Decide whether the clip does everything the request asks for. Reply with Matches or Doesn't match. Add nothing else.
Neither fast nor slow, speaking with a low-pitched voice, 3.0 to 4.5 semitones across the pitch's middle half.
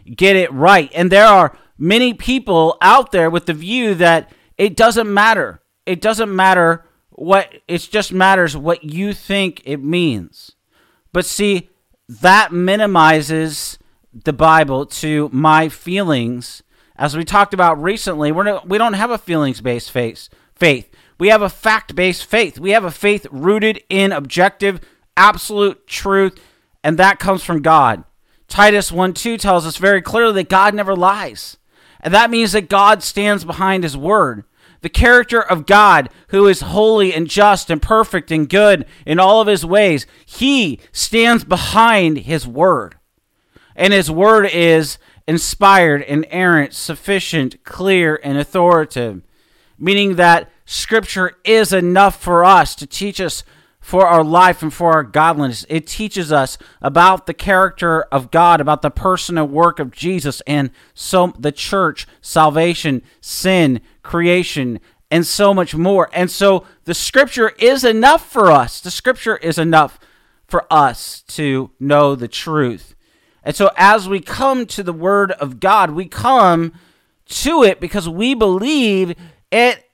Doesn't match